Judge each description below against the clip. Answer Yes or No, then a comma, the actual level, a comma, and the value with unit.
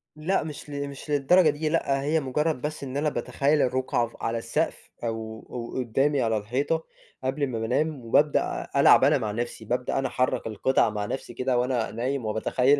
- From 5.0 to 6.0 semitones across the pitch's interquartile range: No, average, 3.7 semitones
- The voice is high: No, low, 130 Hz